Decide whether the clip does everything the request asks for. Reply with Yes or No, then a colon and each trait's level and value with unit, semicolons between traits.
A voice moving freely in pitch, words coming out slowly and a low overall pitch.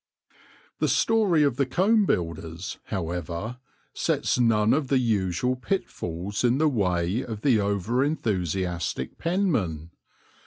Yes: wide, 7.7 semitones; slow, 120 wpm; low, 110 Hz